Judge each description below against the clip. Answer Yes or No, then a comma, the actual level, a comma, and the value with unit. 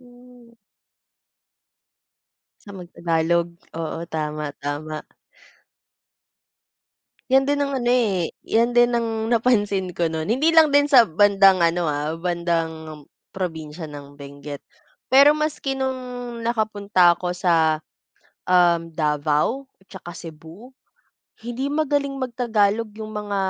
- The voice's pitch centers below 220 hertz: Yes, high, 190 Hz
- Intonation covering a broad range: Yes, wide, 6.9 semitones